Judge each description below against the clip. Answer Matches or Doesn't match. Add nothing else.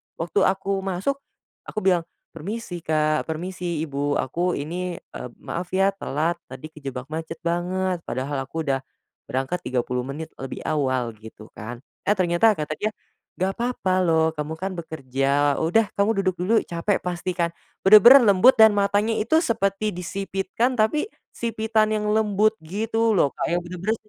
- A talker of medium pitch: Matches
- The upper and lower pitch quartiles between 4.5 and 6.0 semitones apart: Matches